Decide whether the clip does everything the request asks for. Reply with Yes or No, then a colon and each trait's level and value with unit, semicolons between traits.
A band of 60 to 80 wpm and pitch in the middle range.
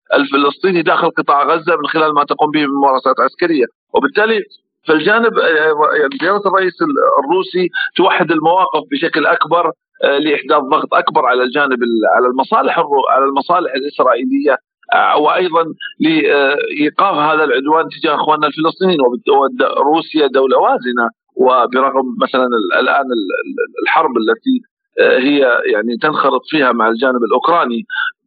No: average, 115 wpm; medium, 180 Hz